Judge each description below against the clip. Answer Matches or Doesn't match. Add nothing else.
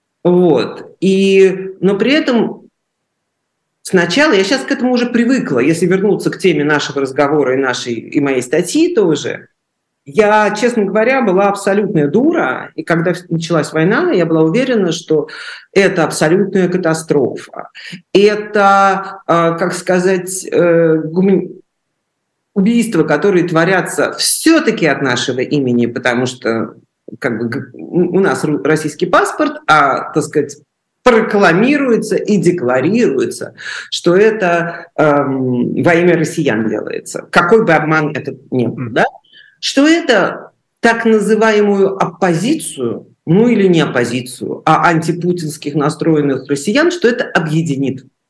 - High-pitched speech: Doesn't match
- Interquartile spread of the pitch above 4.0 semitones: Matches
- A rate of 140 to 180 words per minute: Doesn't match